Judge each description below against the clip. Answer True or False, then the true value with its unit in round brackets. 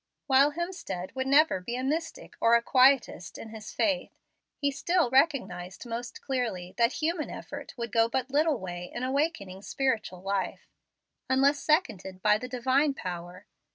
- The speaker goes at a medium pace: True (155 wpm)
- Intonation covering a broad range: True (5.9 semitones)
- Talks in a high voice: True (250 Hz)